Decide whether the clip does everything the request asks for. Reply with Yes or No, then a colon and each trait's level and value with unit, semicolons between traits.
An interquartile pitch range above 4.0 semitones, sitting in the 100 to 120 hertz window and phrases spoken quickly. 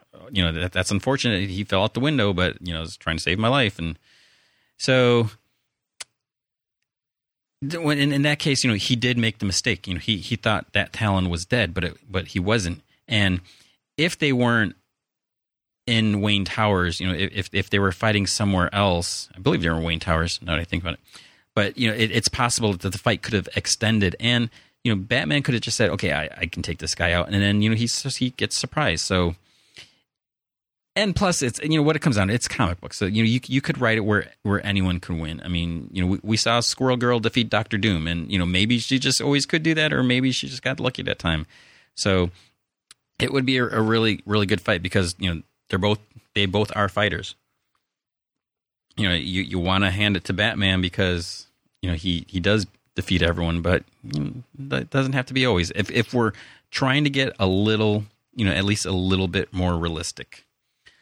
Yes: average, 4.9 semitones; low, 105 Hz; fast, 225 wpm